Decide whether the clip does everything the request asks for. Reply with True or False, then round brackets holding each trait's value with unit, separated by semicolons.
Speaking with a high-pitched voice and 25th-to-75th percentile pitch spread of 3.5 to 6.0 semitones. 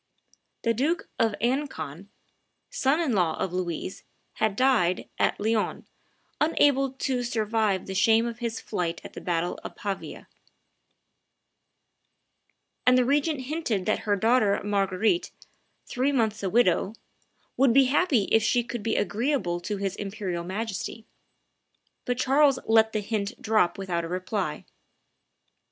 True (220 Hz; 4.8 semitones)